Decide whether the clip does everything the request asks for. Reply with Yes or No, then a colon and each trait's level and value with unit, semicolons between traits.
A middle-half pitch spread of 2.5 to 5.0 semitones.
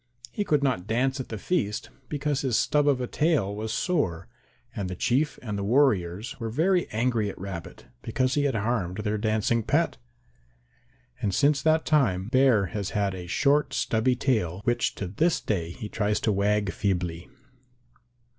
No: wide, 5.5 semitones